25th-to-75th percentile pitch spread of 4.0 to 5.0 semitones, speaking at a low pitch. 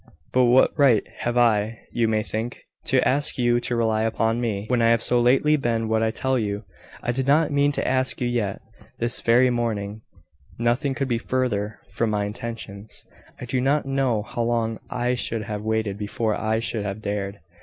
No: narrow, 2.5 semitones; low, 115 Hz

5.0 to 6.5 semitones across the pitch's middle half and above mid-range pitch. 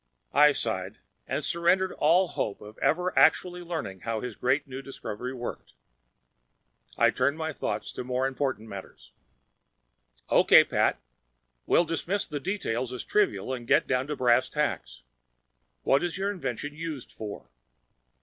No: wide, 5.4 semitones; low, 135 Hz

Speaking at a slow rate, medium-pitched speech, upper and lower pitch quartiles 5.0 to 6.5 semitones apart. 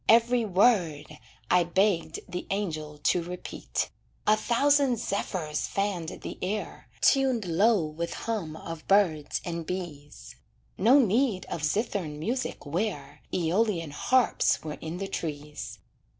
Yes: slow, 125 wpm; medium, 180 Hz; wide, 5.4 semitones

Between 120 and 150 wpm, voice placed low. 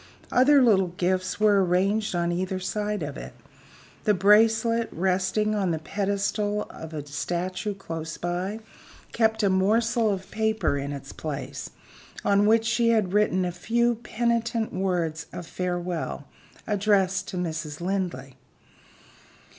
No: slow, 135 wpm; high, 195 Hz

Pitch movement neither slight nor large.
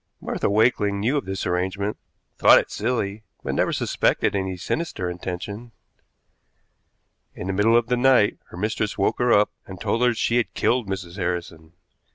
Yes: average, 3.9 semitones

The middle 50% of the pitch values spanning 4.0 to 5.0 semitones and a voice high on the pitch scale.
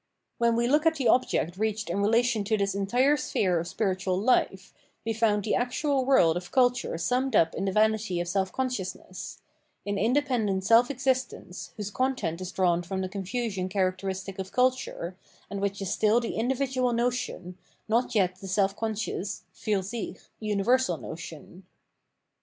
Yes: average, 4.6 semitones; high, 210 Hz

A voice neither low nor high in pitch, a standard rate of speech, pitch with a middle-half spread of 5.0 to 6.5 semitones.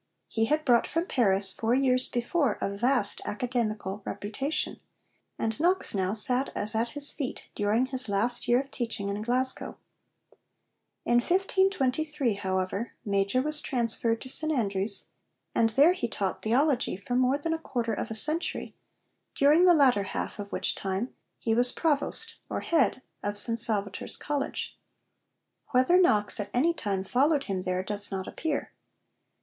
No: high, 240 Hz; average, 155 wpm; wide, 5.5 semitones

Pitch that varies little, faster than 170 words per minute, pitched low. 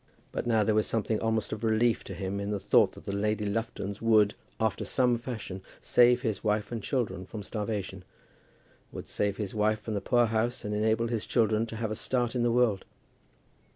Yes: narrow, 2.0 semitones; average, 200 wpm; low, 110 Hz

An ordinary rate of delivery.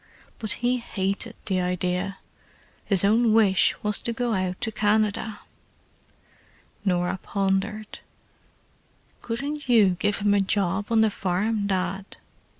No: slow, 125 wpm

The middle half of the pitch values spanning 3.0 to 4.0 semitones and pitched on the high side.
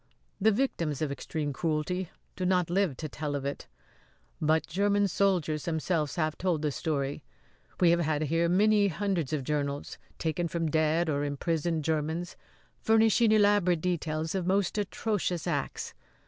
No: average, 3.6 semitones; medium, 165 Hz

